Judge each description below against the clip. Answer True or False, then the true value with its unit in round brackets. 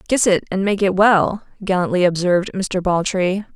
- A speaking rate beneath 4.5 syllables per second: False (5.0 syllables/s)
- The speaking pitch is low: False (190 Hz)